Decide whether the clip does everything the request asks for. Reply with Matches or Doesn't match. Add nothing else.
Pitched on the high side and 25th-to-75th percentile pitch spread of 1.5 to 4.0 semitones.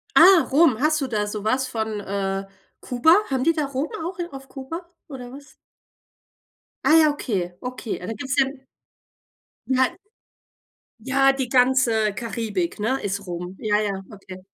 Doesn't match